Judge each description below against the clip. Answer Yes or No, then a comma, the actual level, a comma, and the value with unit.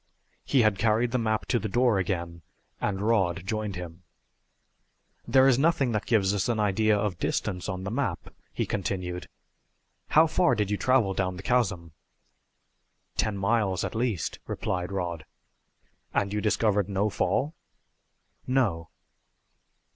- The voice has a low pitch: Yes, low, 105 Hz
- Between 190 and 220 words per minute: No, average, 145 wpm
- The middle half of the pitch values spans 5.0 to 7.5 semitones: No, average, 3.7 semitones